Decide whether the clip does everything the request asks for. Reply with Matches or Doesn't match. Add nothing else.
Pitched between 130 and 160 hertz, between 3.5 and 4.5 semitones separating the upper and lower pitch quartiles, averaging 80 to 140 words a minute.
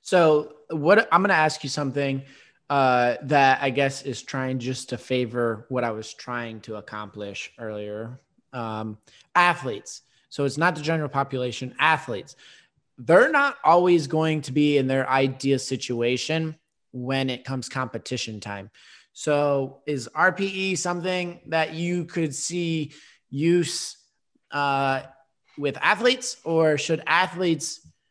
Matches